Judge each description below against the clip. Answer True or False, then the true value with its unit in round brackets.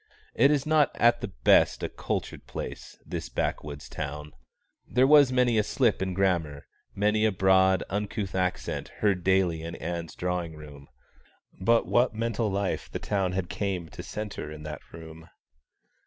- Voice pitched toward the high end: False (95 Hz)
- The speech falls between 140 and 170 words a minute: True (160 wpm)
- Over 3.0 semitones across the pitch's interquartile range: True (4.8 semitones)